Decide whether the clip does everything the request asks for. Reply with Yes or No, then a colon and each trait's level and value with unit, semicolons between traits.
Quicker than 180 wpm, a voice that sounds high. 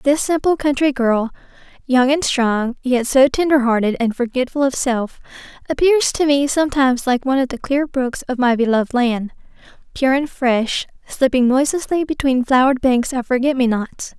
No: average, 175 wpm; very high, 260 Hz